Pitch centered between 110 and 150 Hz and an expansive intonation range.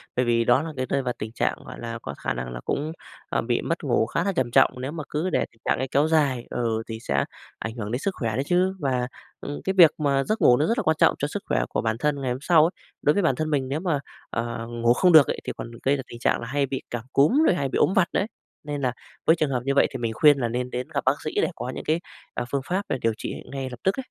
No: low, 135 Hz; average, 4.6 semitones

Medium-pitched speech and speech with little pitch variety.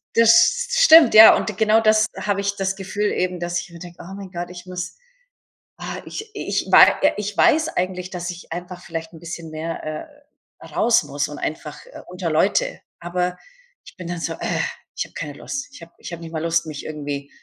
No: medium, 180 Hz; average, 3.6 semitones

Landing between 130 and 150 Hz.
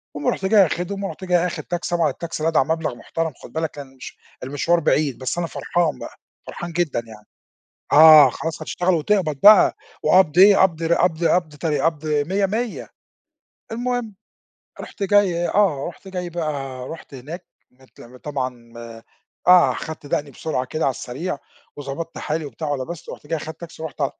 No: medium, 160 Hz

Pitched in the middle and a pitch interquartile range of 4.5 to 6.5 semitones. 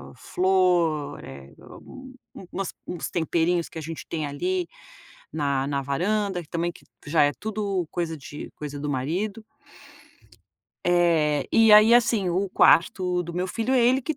Yes: medium, 175 Hz; average, 4.9 semitones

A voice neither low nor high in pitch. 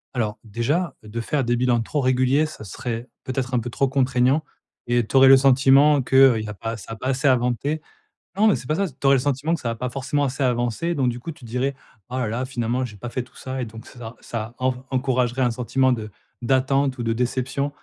No: low, 130 Hz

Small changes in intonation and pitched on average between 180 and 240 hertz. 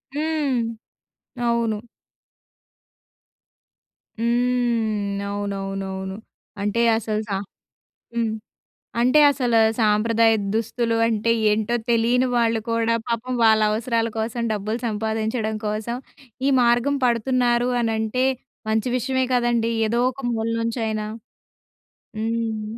Yes: narrow, 1.7 semitones; high, 230 Hz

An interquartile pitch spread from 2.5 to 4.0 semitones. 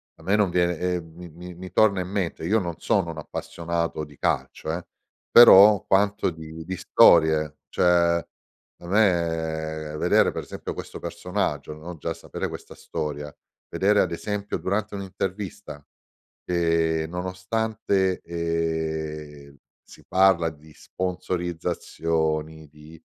Yes: average, 2.9 semitones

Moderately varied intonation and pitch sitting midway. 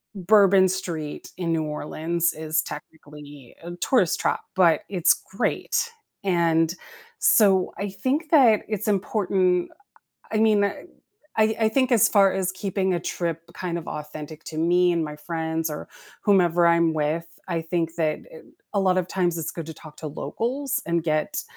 Yes: average, 3.5 semitones; medium, 175 Hz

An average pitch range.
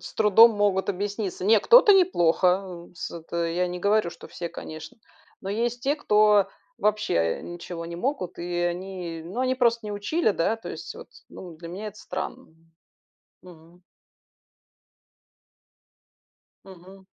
Yes: average, 3.9 semitones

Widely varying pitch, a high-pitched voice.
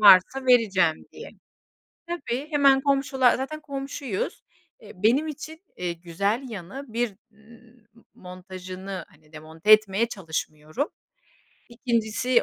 Yes: wide, 6.4 semitones; high, 225 Hz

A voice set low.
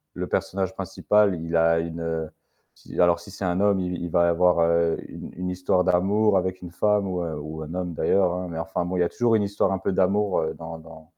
Yes: very low, 90 Hz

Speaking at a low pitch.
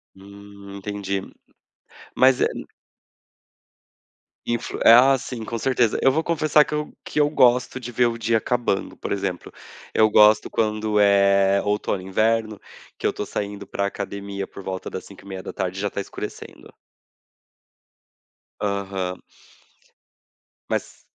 Yes: low, 105 Hz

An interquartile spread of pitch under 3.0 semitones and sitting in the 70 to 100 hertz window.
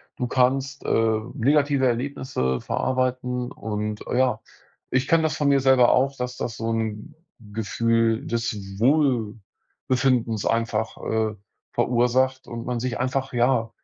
No: narrow, 2.6 semitones; low, 125 Hz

